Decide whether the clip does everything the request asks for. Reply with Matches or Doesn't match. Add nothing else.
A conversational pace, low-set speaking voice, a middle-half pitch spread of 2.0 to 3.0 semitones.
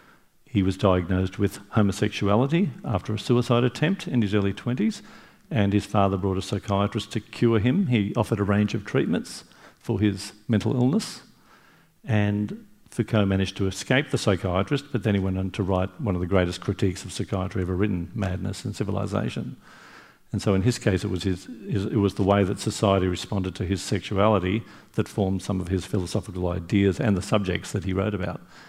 Matches